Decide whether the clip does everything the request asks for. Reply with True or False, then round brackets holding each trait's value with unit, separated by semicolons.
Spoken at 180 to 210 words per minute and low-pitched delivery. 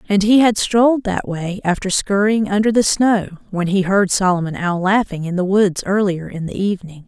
False (205 wpm; 195 Hz)